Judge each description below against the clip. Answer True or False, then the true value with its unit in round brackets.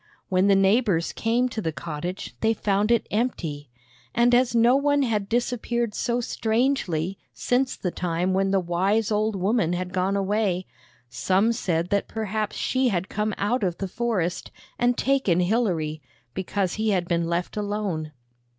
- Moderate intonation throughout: True (4.4 semitones)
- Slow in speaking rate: False (160 wpm)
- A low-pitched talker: False (200 Hz)